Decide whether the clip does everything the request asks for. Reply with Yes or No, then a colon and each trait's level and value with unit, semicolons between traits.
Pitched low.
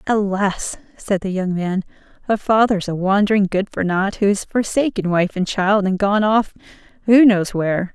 No: high, 200 Hz